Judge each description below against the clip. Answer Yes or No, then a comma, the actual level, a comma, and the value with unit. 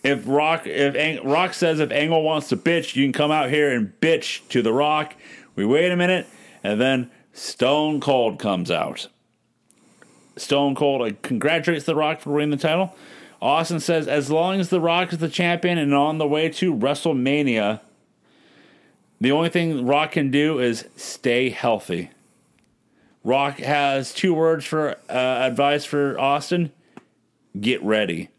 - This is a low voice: No, medium, 150 Hz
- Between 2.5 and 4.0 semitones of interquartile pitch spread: Yes, average, 3.1 semitones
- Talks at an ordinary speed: Yes, average, 160 wpm